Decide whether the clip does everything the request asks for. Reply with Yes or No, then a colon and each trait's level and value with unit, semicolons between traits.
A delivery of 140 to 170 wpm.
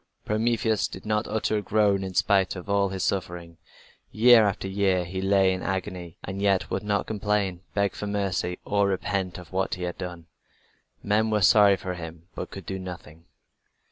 No: average, 195 wpm